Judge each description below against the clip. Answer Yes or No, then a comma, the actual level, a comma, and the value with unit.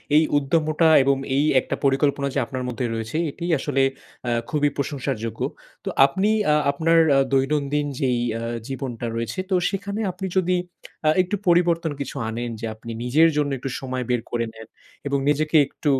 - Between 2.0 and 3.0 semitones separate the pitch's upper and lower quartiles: No, average, 3.9 semitones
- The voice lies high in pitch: No, medium, 140 Hz